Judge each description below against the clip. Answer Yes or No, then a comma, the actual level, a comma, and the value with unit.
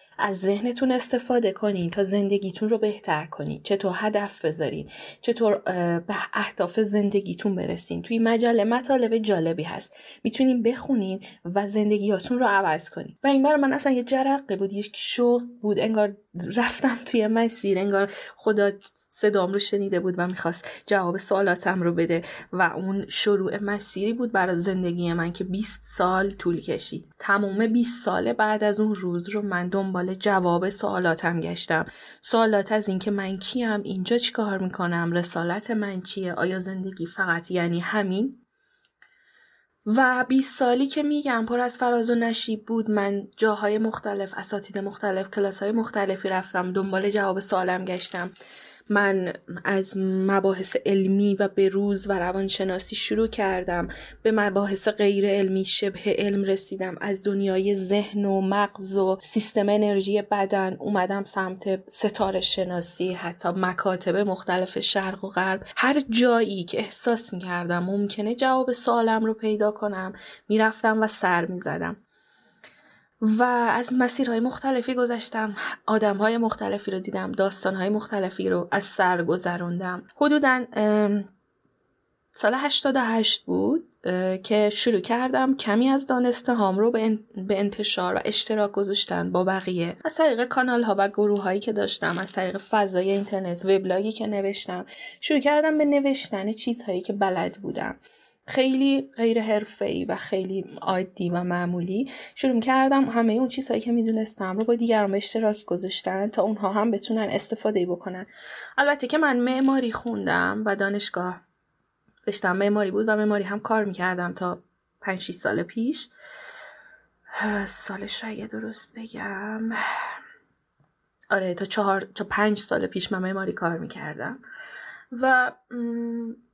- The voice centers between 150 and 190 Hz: No, high, 205 Hz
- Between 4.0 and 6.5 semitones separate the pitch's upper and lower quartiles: No, average, 3.2 semitones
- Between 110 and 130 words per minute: No, average, 140 wpm